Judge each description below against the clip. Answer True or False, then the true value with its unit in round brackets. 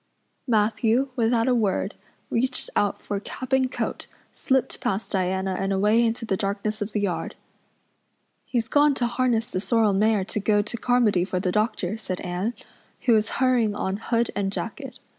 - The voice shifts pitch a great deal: False (3.3 semitones)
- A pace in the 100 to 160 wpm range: False (175 wpm)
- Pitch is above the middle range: True (220 Hz)